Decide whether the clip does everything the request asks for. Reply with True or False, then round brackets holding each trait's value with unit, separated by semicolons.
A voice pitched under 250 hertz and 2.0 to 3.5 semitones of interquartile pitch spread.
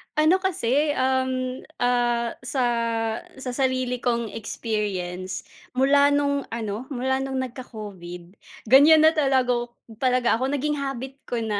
False (255 Hz; 2.8 semitones)